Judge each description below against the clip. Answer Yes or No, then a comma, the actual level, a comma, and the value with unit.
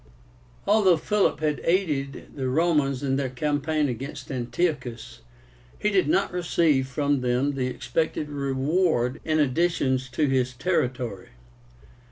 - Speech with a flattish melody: No, average, 3.7 semitones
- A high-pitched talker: No, medium, 140 Hz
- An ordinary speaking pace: No, slow, 125 wpm